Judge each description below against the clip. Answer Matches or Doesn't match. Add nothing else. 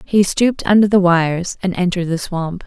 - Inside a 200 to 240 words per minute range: Matches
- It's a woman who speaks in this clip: Matches